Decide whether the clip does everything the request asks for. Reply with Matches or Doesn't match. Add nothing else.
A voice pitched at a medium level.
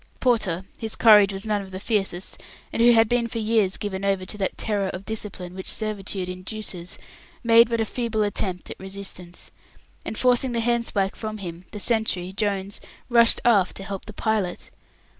Doesn't match